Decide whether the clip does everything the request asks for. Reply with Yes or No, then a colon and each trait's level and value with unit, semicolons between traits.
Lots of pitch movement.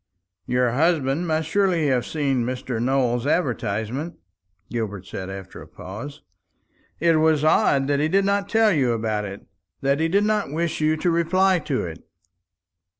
Yes: wide, 5.7 semitones